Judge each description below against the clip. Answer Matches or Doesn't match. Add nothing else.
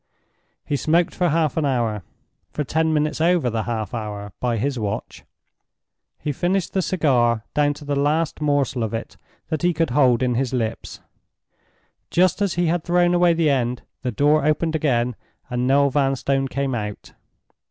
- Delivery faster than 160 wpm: Matches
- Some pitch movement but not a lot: Matches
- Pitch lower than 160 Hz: Matches